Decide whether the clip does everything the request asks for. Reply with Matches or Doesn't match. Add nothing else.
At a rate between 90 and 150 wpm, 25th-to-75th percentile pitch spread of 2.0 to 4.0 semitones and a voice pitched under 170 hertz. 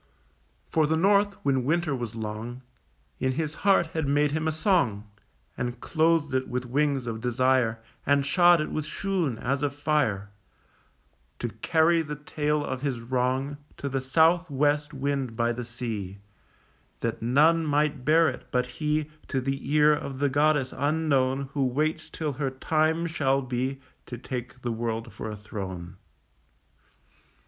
Doesn't match